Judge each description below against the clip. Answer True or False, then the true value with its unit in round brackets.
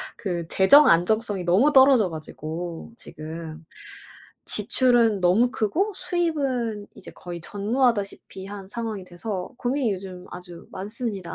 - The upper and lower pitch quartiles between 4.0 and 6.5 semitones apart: True (5.3 semitones)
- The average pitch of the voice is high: True (205 Hz)